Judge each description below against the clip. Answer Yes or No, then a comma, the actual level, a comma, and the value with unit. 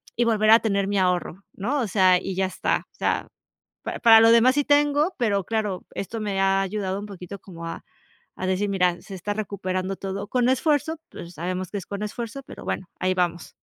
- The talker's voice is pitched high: Yes, high, 200 Hz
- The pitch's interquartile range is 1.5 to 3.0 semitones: No, average, 3.4 semitones